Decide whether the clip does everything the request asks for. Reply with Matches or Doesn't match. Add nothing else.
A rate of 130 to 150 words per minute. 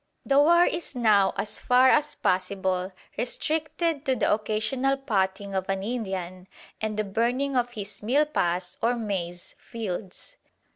Matches